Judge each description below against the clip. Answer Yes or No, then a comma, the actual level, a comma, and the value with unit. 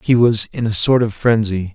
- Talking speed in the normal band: No, fast, 240 wpm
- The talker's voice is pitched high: No, low, 110 Hz